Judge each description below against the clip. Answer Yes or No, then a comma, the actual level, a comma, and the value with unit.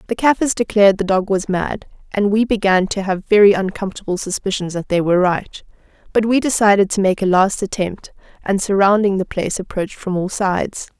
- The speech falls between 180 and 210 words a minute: Yes, average, 190 wpm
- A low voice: No, high, 195 Hz